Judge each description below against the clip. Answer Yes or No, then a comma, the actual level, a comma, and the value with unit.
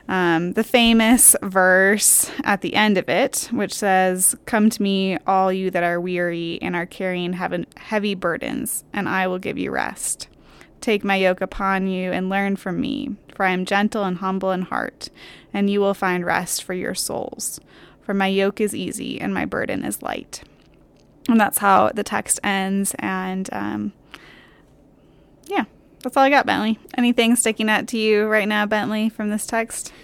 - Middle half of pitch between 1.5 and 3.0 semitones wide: Yes, average, 2.7 semitones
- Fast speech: No, average, 180 wpm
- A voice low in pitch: No, high, 200 Hz